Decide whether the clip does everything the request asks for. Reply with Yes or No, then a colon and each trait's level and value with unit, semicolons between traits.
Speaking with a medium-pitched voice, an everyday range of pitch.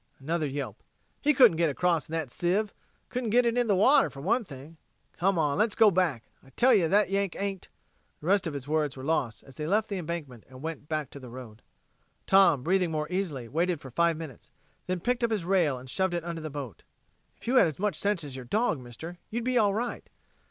No: medium, 170 Hz; wide, 5.8 semitones